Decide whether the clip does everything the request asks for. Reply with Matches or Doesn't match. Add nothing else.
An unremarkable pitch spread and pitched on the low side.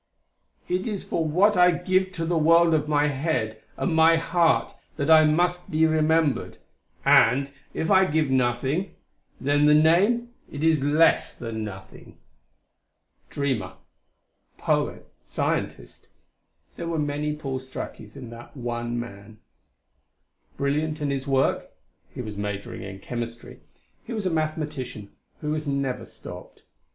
Doesn't match